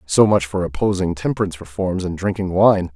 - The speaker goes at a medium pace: Yes, average, 185 wpm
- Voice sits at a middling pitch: No, very low, 95 Hz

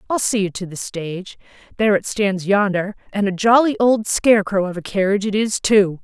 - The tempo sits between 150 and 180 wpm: No, average, 200 wpm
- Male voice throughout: No, female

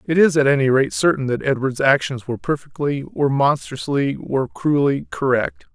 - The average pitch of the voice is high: No, medium, 140 Hz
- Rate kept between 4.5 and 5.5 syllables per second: Yes, 5.3 syllables/s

